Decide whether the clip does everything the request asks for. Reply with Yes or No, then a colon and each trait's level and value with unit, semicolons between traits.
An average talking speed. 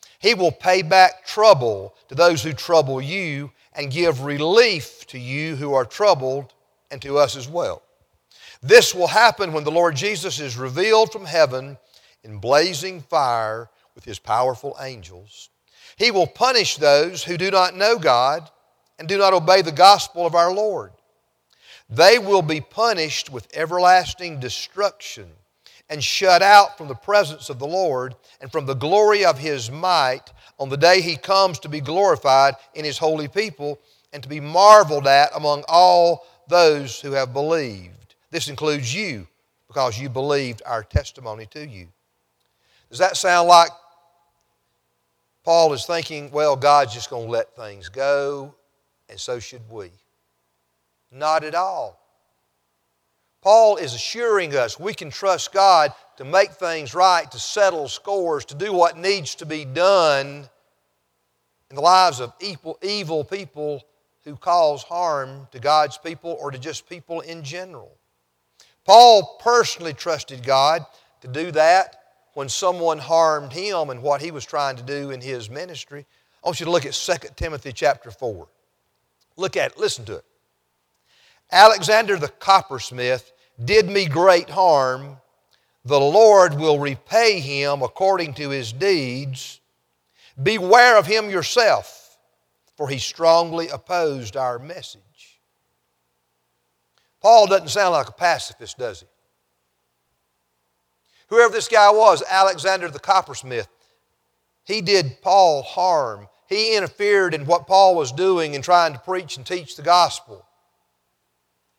Yes: average, 145 wpm